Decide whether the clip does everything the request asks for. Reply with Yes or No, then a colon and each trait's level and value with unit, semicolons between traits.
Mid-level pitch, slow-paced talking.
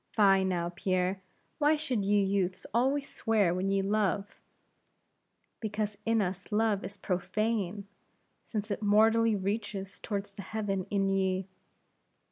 No: high, 200 Hz; slow, 130 wpm